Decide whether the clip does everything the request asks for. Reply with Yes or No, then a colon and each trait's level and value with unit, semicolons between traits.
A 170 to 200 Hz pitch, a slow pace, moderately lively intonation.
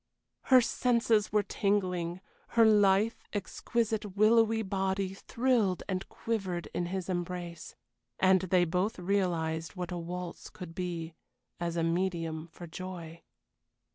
Yes: medium, 185 Hz; slow, 125 wpm; average, 3.1 semitones